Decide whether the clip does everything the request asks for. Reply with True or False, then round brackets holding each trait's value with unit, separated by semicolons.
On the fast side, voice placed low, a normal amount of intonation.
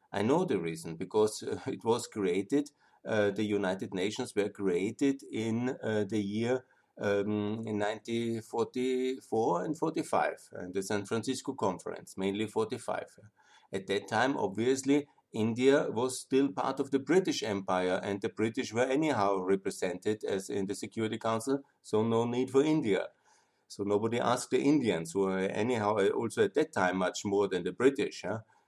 False (160 wpm; 110 Hz; 4.1 semitones)